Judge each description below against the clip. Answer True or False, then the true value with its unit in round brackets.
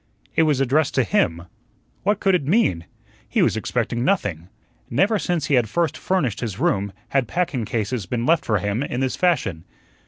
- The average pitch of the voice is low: True (130 Hz)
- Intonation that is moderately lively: False (8.3 semitones)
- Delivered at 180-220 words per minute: True (185 wpm)